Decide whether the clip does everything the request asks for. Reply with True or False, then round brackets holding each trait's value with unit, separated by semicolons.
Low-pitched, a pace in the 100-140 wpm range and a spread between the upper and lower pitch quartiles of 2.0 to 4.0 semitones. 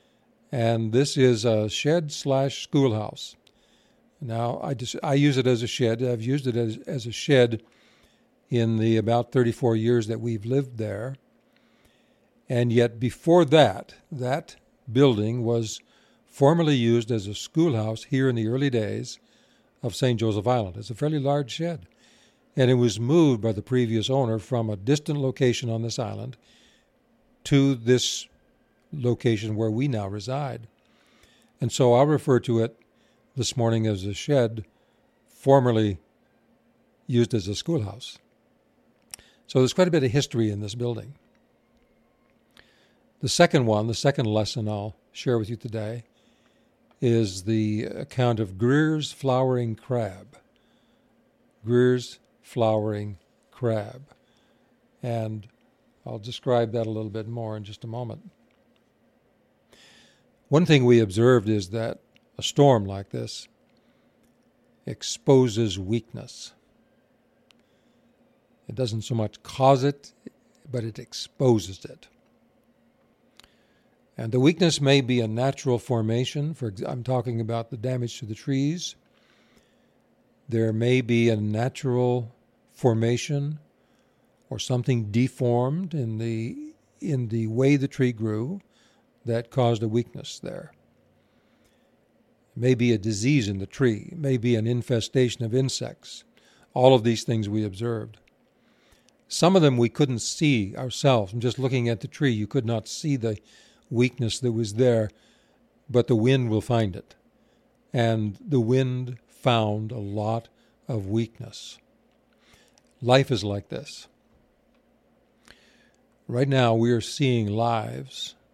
True (120 Hz; 135 wpm; 2.9 semitones)